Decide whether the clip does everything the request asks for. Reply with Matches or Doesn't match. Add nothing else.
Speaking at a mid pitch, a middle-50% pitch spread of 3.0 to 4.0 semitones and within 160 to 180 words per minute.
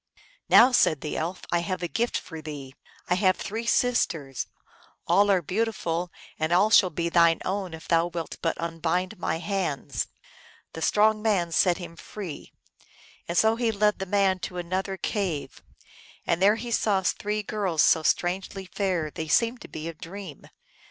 Matches